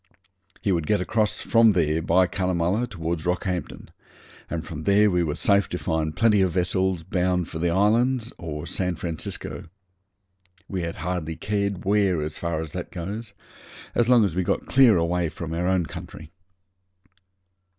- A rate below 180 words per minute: Yes, average, 165 wpm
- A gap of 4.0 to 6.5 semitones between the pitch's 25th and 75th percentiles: No, average, 3.3 semitones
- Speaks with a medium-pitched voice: No, very low, 90 Hz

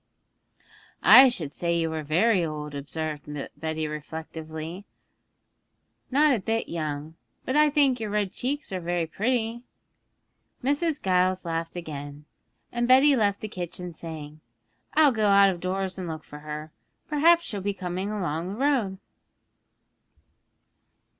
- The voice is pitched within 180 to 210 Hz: Yes, medium, 185 Hz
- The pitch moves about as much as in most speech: No, wide, 6.4 semitones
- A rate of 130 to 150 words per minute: Yes, average, 140 wpm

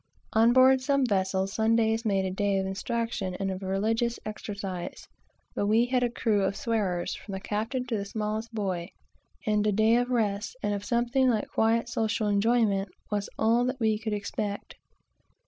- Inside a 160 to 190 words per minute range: Yes, average, 180 wpm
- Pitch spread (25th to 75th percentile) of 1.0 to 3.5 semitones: Yes, average, 2.7 semitones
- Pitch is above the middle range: Yes, high, 215 Hz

